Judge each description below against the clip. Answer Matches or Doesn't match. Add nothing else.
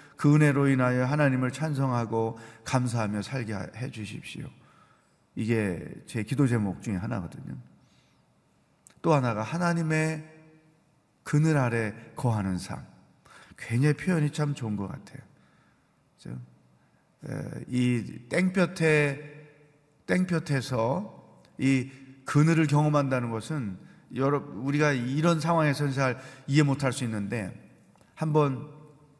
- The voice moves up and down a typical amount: Matches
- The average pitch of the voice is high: Doesn't match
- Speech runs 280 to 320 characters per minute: Doesn't match